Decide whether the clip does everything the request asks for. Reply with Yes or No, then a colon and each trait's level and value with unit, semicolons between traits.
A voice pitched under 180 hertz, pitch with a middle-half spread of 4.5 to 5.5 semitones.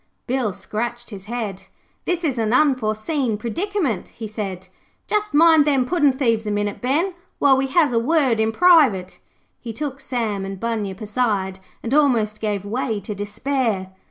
No: high, 235 Hz; average, 5.0 semitones